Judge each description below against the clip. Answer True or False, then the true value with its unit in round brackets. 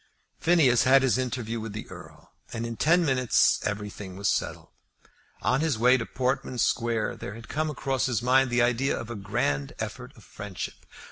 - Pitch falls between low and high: False (120 Hz)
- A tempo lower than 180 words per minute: False (185 wpm)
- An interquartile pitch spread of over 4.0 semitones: False (3.1 semitones)